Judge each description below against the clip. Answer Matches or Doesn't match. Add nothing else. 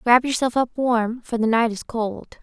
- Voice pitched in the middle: Doesn't match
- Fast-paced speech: Matches